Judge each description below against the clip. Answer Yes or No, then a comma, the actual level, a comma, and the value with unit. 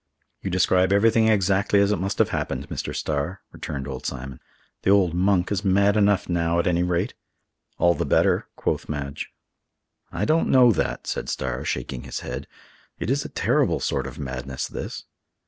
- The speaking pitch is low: Yes, very low, 90 Hz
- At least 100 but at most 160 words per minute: No, average, 180 wpm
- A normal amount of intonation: No, wide, 6.0 semitones